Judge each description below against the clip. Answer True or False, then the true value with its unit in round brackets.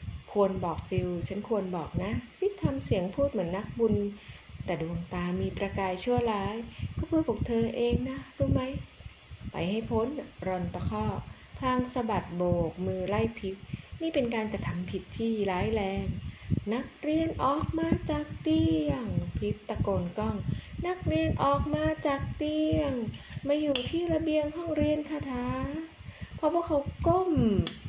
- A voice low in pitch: False (225 Hz)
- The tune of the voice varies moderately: False (8.4 semitones)